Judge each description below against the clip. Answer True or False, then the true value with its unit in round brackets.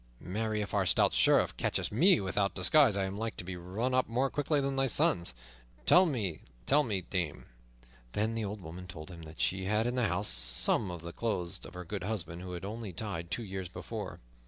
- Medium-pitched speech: False (100 Hz)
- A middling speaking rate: False (220 wpm)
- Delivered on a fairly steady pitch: False (4.2 semitones)